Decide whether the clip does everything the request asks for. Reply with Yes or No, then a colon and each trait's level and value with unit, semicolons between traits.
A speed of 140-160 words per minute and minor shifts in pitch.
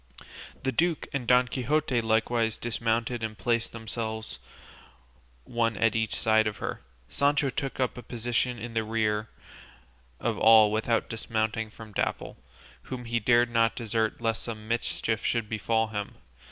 Yes: average, 150 wpm; narrow, 1.4 semitones